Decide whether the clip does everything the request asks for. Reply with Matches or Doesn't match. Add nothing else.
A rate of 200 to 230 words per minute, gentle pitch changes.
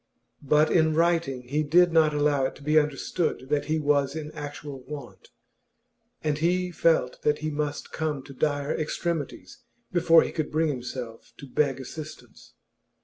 Doesn't match